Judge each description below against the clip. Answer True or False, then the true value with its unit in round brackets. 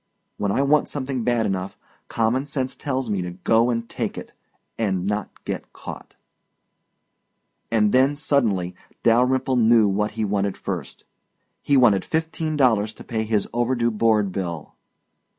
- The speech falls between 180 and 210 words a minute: False (150 wpm)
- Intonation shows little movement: False (4.1 semitones)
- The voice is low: True (115 Hz)